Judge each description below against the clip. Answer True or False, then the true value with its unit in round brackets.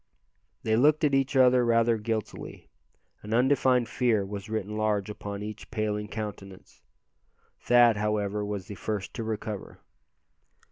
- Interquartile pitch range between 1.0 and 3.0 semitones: True (2.5 semitones)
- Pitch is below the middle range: True (110 Hz)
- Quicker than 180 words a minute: False (135 wpm)